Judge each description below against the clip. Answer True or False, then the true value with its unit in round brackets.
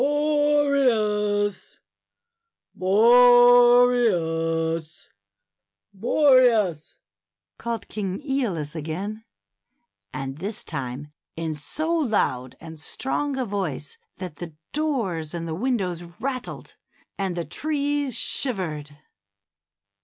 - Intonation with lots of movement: True (7.8 semitones)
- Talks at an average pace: False (80 wpm)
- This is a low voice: False (205 Hz)